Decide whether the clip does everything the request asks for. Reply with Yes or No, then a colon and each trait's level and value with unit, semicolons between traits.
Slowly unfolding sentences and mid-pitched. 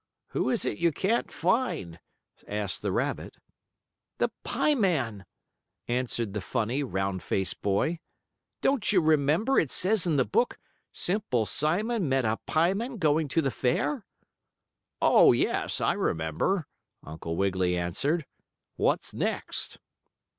Yes: slow, 130 wpm; medium, 145 Hz